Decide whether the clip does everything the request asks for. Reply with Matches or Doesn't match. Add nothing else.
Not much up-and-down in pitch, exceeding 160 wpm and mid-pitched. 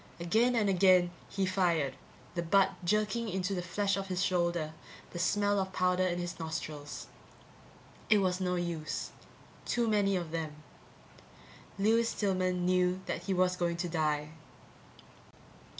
Doesn't match